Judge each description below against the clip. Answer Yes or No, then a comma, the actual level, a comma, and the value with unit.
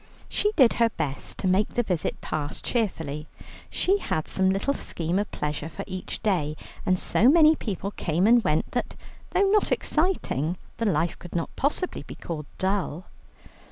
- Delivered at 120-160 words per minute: No, average, 170 wpm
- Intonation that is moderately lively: No, wide, 6.7 semitones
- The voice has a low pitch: No, high, 190 Hz